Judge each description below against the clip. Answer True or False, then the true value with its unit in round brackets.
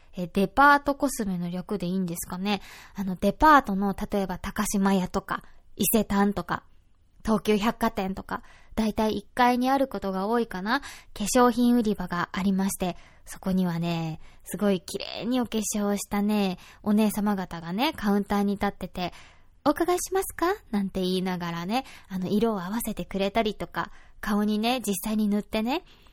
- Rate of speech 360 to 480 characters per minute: False (335 characters per minute)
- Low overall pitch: False (205 Hz)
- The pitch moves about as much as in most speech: True (3.2 semitones)